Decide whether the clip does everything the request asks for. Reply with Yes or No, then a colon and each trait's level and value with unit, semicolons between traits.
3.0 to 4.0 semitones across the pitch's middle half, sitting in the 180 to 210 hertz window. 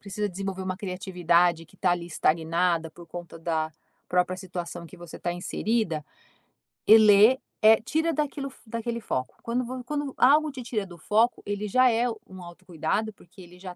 No: average, 5.0 semitones; high, 190 Hz